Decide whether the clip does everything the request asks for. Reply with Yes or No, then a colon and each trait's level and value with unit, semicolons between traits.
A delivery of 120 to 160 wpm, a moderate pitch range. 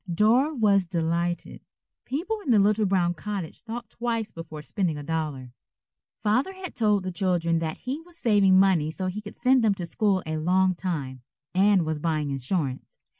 No: average, 175 wpm; average, 4.8 semitones